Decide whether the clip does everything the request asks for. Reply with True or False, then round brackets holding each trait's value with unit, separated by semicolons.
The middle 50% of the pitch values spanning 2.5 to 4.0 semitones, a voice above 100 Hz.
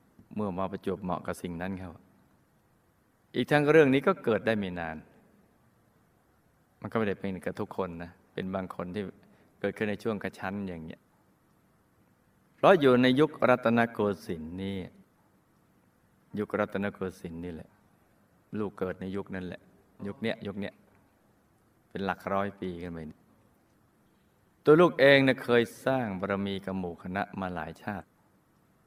False (3.5 semitones; 95 Hz)